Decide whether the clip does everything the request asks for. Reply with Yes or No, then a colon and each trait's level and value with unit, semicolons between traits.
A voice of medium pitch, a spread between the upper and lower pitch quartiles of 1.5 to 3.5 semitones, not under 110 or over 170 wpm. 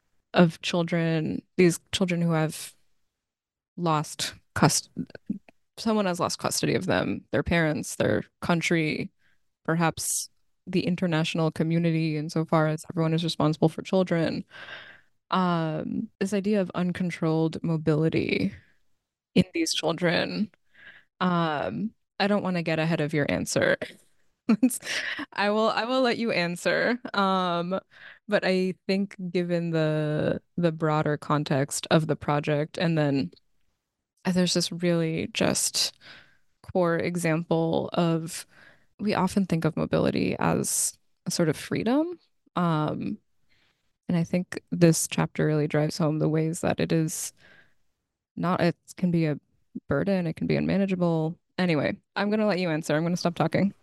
Yes: medium, 170 Hz; average, 2.8 semitones; slow, 135 wpm